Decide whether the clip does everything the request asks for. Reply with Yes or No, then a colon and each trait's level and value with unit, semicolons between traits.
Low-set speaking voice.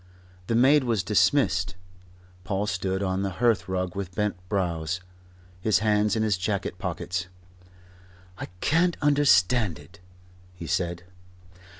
Yes: very low, 95 Hz